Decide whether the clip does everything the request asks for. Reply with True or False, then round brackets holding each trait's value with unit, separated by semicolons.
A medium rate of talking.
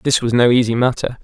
False (245 wpm)